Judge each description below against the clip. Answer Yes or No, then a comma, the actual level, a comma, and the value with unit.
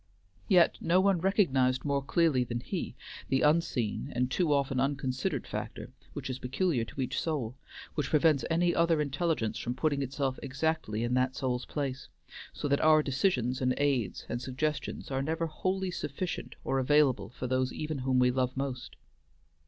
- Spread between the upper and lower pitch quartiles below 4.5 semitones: Yes, average, 3.5 semitones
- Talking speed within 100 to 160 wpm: No, average, 170 wpm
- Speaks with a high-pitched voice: No, low, 135 Hz